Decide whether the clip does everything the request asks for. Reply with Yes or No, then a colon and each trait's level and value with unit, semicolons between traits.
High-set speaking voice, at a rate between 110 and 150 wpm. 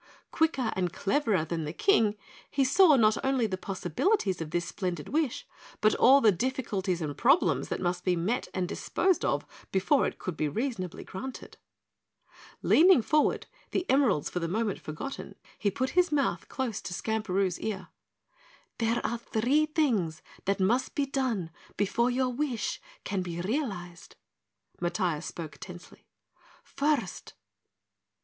Yes: high, 215 Hz; average, 145 wpm